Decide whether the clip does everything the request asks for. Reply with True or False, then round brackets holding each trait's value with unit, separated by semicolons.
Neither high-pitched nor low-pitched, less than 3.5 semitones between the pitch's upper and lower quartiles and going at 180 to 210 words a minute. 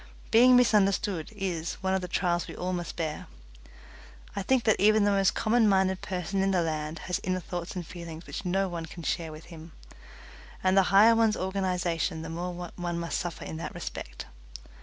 True (180 Hz; 2.6 semitones; 195 wpm)